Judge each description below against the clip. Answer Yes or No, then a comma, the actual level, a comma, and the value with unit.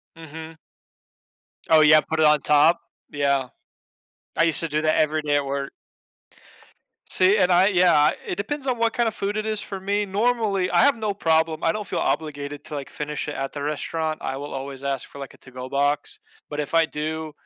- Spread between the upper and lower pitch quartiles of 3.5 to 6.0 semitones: Yes, average, 4.7 semitones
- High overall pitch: No, medium, 155 Hz